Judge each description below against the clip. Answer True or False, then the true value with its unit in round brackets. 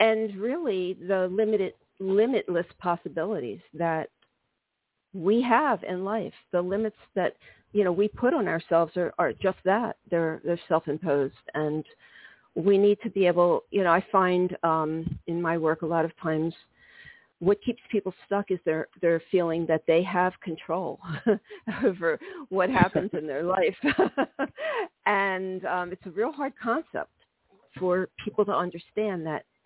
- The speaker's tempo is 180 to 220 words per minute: False (145 wpm)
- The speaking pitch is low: False (185 Hz)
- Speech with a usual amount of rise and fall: True (4.1 semitones)